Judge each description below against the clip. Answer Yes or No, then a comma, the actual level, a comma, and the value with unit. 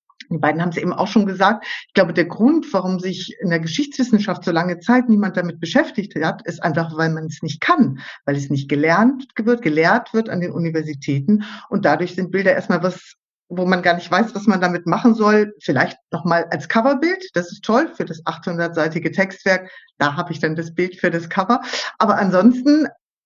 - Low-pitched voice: No, medium, 185 Hz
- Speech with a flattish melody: No, average, 4.2 semitones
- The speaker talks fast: Yes, fast, 205 wpm